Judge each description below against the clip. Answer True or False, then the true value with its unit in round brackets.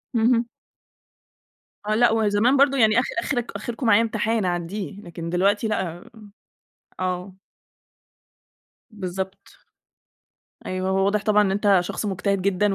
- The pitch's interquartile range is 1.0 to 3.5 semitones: True (3.0 semitones)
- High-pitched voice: True (205 Hz)